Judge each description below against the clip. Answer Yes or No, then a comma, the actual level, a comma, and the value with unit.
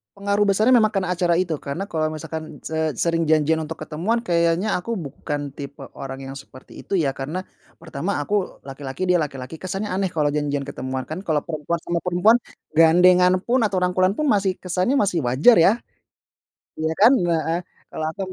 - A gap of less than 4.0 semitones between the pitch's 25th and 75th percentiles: No, average, 4.3 semitones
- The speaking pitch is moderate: Yes, medium, 170 Hz